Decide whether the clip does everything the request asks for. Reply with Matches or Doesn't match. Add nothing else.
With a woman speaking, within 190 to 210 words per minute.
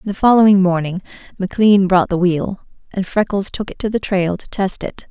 Matches